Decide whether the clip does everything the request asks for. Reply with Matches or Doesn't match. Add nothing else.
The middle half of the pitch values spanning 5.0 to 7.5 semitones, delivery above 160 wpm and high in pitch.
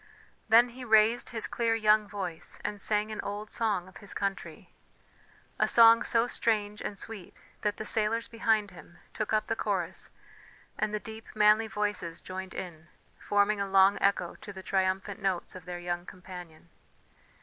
Doesn't match